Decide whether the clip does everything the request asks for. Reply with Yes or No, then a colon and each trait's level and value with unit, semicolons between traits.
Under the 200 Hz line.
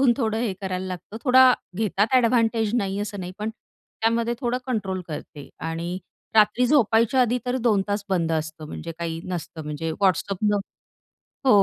No: high, 205 Hz